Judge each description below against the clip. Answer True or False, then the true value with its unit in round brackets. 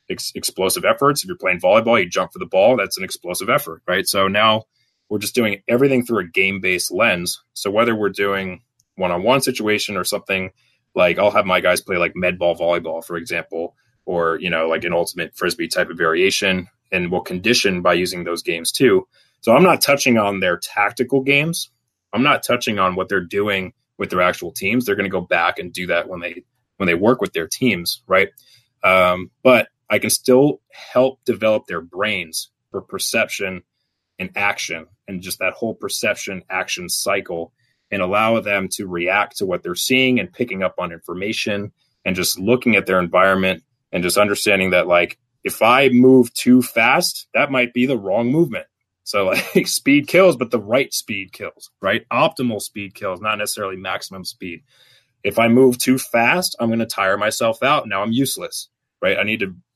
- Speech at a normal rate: True (190 wpm)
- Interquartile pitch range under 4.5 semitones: False (5.3 semitones)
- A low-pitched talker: True (105 Hz)